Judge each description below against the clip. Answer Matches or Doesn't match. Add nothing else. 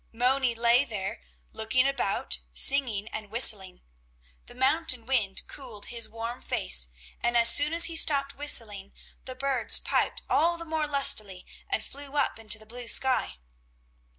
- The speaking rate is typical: Matches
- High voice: Matches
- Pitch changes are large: Doesn't match